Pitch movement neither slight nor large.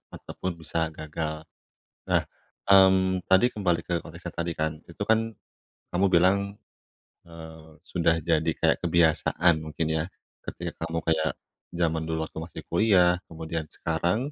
No: narrow, 2.0 semitones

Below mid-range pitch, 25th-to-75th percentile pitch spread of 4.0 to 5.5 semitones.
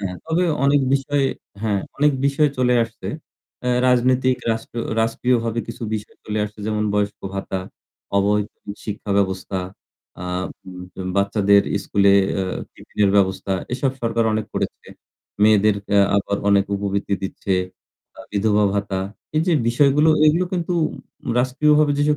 Yes: low, 110 Hz; average, 4.5 semitones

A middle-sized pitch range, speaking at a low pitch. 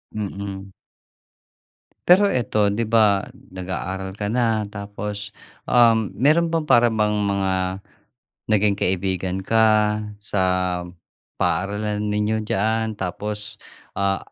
No: narrow, 2.2 semitones; low, 105 Hz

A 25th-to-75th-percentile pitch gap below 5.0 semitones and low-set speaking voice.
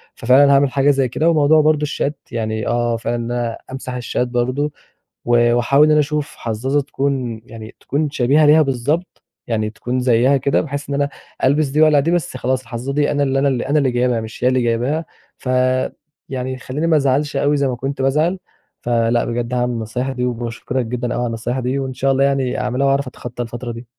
Yes: average, 2.8 semitones; low, 130 Hz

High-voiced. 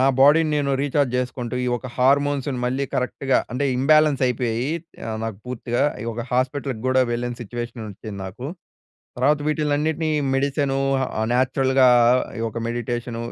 No: low, 130 Hz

